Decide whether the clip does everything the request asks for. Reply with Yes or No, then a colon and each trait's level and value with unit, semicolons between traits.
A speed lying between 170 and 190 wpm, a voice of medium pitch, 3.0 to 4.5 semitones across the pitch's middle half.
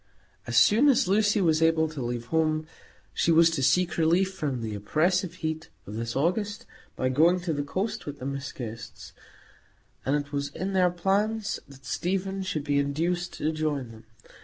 No: average, 185 wpm; medium, 160 Hz; average, 4.9 semitones